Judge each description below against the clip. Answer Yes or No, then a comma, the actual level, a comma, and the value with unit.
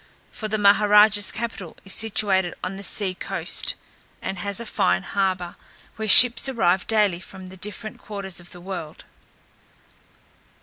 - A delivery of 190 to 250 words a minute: No, average, 155 wpm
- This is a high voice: Yes, high, 200 Hz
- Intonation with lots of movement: No, average, 2.7 semitones